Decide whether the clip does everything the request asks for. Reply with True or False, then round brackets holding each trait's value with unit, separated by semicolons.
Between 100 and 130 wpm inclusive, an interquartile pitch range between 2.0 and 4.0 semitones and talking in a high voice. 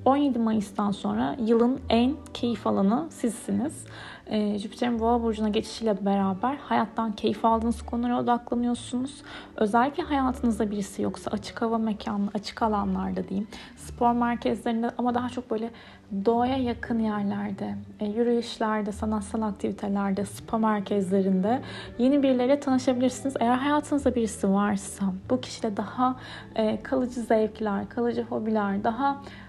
True (120 wpm; 2.8 semitones; 230 Hz)